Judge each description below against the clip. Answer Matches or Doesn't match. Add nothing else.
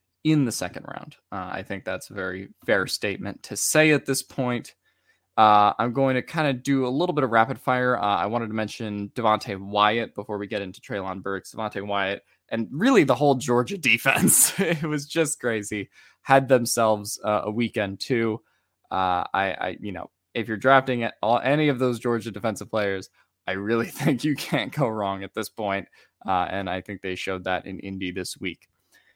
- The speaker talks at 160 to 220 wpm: Matches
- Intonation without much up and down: Doesn't match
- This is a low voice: Matches